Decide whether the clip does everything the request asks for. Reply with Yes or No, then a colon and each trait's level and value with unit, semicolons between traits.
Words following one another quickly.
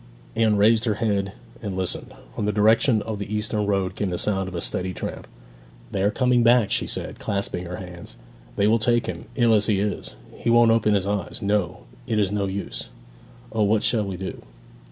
Yes: fast, 210 wpm